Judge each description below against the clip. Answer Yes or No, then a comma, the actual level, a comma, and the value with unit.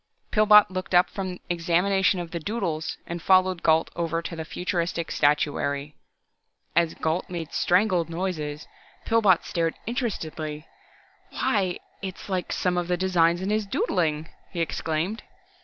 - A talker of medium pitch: Yes, medium, 175 Hz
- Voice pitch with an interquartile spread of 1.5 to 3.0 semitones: Yes, narrow, 2.5 semitones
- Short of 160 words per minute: Yes, average, 140 wpm